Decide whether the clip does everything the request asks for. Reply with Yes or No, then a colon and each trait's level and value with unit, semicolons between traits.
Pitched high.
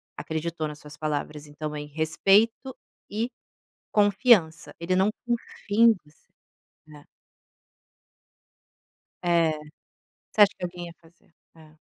No: medium, 170 Hz